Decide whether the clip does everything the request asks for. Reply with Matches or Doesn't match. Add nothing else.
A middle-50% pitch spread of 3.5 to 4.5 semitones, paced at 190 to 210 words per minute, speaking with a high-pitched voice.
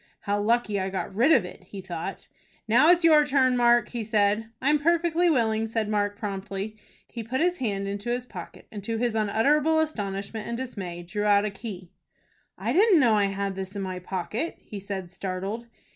Matches